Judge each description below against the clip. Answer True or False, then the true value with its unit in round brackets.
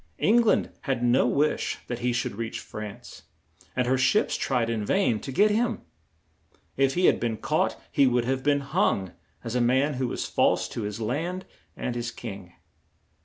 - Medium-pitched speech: False (125 Hz)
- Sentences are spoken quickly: False (185 wpm)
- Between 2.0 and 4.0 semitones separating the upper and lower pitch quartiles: True (3.4 semitones)